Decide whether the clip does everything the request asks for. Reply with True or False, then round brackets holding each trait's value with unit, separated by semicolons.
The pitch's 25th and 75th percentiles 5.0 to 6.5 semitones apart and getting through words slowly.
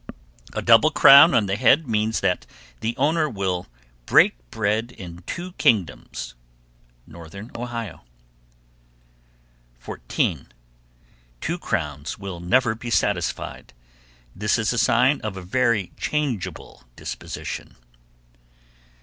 True (5.3 semitones; 105 wpm)